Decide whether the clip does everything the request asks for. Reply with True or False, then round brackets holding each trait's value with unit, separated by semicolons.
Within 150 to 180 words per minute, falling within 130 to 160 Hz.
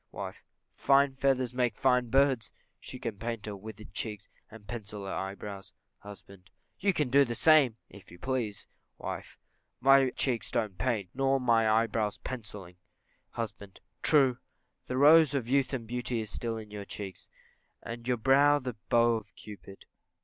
False (165 wpm; 115 Hz)